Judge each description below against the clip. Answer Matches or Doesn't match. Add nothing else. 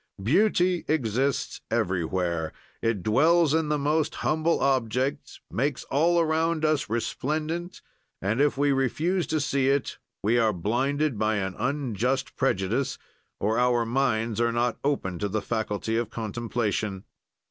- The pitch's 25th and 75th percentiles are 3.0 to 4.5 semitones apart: Doesn't match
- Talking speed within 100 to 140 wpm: Matches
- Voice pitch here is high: Doesn't match